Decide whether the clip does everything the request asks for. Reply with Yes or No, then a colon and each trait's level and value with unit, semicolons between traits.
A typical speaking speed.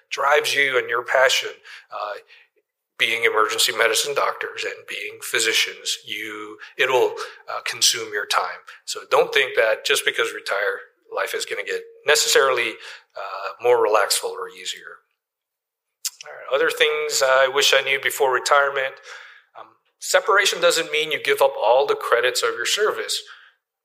Yes: average, 150 wpm